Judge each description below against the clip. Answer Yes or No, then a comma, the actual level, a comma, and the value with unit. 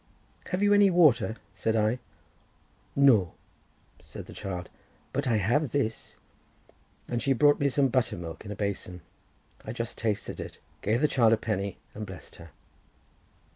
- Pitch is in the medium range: No, low, 115 Hz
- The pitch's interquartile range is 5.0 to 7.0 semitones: Yes, wide, 5.5 semitones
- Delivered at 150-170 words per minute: Yes, average, 160 wpm